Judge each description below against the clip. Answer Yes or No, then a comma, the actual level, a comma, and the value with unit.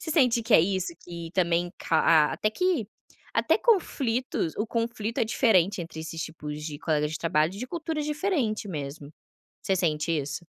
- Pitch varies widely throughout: Yes, wide, 6.8 semitones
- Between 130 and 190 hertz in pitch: Yes, medium, 185 Hz